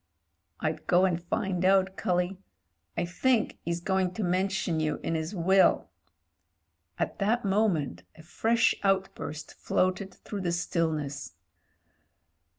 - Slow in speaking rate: Yes, slow, 130 wpm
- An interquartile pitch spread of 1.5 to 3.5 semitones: Yes, narrow, 2.5 semitones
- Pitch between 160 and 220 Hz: Yes, medium, 185 Hz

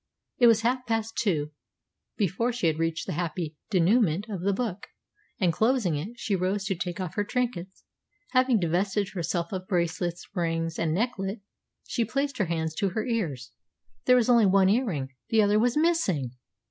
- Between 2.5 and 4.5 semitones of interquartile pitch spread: No, average, 5.2 semitones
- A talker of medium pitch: No, high, 195 Hz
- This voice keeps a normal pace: Yes, average, 180 wpm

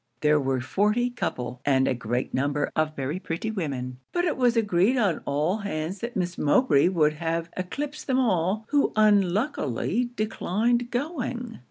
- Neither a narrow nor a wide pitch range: No, wide, 8.0 semitones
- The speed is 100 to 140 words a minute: No, average, 160 wpm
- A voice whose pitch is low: No, medium, 185 Hz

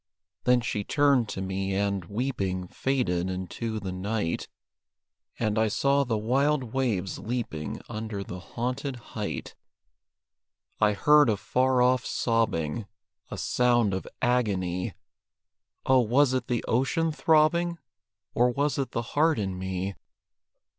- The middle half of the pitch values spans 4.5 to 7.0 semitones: Yes, average, 5.1 semitones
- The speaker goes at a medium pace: No, slow, 130 wpm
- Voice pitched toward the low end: Yes, low, 115 Hz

